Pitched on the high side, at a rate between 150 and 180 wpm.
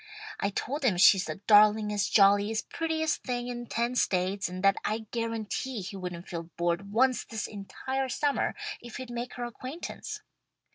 Yes: high, 220 Hz; average, 160 wpm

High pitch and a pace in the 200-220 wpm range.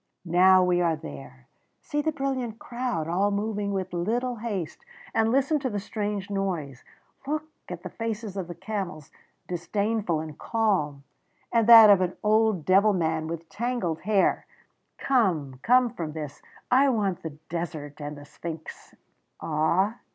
No: high, 195 Hz; average, 150 wpm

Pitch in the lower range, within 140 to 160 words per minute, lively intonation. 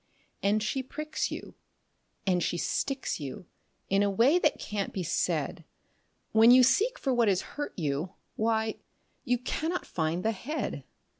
No: high, 220 Hz; average, 155 wpm; wide, 6.0 semitones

